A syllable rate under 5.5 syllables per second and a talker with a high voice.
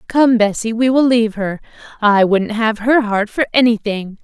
Yes: 4.8 syllables/s; high, 225 Hz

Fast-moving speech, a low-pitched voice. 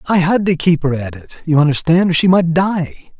No: fast, 245 wpm; medium, 165 Hz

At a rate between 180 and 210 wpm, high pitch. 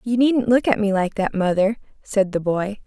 No: fast, 230 wpm; high, 210 Hz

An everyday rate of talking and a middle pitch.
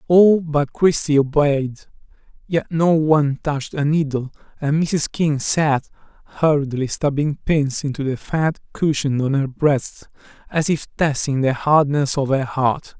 Yes: average, 150 wpm; medium, 145 Hz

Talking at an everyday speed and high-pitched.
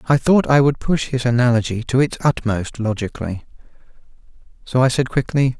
No: average, 160 wpm; low, 125 Hz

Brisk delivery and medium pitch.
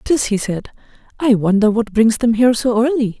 No: fast, 225 wpm; high, 230 Hz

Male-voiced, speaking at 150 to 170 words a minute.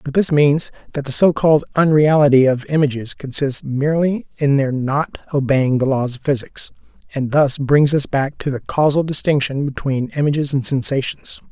Yes: male; average, 165 wpm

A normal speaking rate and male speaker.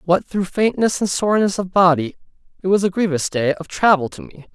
No: fast, 210 wpm; male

